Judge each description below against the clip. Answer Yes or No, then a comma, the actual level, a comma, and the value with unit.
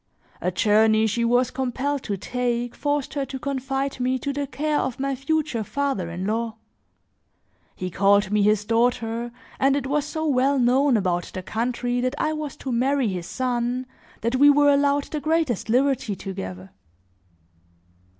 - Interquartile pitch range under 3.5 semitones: No, average, 4.2 semitones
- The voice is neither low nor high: No, very high, 250 Hz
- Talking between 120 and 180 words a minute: Yes, average, 165 wpm